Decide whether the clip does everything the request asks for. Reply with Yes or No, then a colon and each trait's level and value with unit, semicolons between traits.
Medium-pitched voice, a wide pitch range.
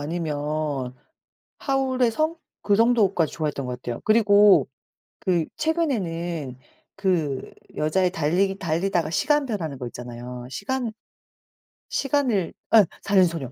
Yes: medium, 175 Hz; wide, 6.8 semitones